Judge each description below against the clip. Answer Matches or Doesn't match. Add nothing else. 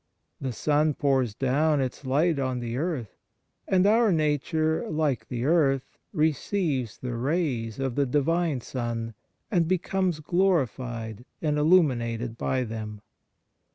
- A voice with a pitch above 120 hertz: Matches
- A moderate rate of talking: Doesn't match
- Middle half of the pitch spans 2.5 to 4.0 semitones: Doesn't match